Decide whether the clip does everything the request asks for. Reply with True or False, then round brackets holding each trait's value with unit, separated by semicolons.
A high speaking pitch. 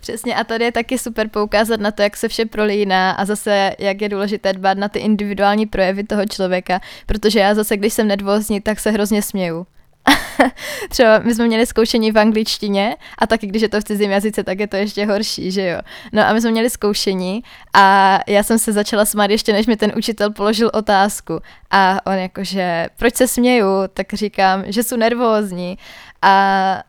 True (210 Hz)